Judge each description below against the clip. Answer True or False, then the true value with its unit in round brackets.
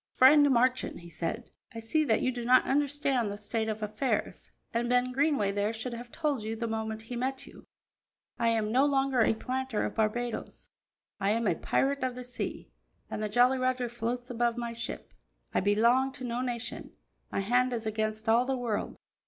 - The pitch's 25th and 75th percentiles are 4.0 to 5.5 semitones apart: False (2.6 semitones)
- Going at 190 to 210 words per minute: True (195 wpm)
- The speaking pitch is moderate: False (240 Hz)